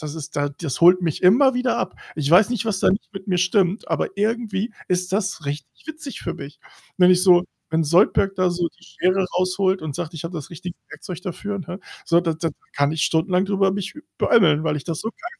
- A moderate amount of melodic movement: Yes, average, 3.4 semitones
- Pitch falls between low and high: Yes, medium, 180 Hz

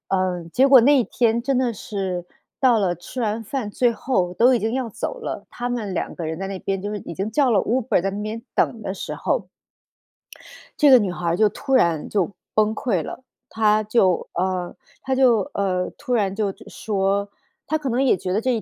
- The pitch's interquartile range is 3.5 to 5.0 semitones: Yes, average, 4.5 semitones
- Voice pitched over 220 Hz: No, high, 215 Hz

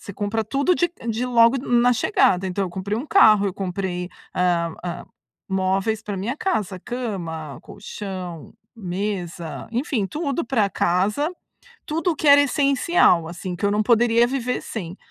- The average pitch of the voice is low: No, high, 210 Hz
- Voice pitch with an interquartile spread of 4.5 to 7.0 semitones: Yes, average, 5.3 semitones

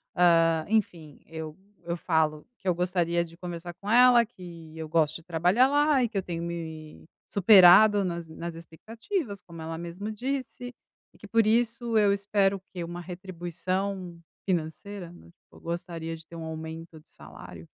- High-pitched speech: No, medium, 175 Hz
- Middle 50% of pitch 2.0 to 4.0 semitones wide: Yes, average, 3.7 semitones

